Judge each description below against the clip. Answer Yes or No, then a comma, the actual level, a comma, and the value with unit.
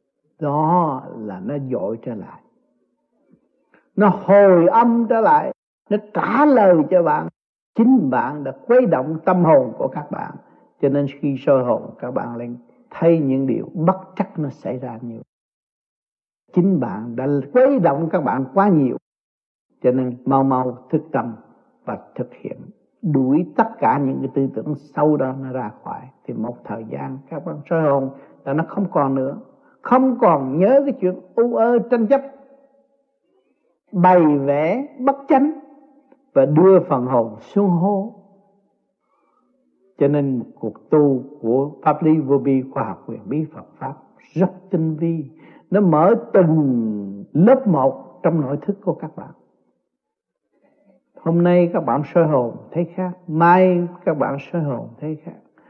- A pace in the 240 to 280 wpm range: No, slow, 165 wpm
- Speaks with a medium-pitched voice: Yes, medium, 170 Hz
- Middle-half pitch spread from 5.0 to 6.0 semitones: No, wide, 6.5 semitones